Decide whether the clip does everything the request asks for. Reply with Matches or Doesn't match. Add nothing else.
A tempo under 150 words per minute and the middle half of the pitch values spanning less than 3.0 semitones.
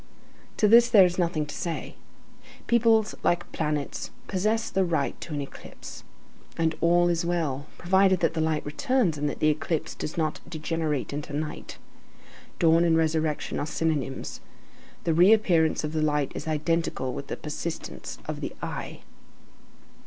Doesn't match